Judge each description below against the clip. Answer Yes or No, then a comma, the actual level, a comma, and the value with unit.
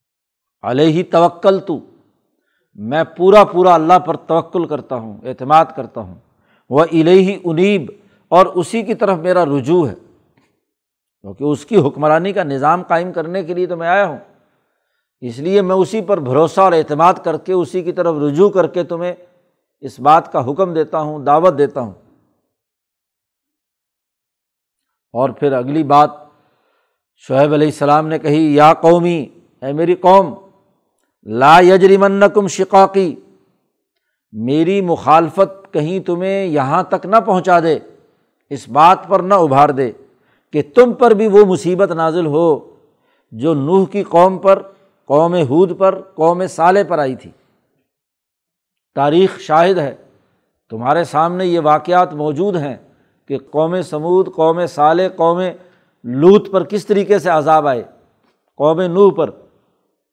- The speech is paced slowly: No, average, 145 wpm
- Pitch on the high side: No, medium, 175 Hz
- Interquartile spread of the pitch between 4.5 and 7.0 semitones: No, average, 4.0 semitones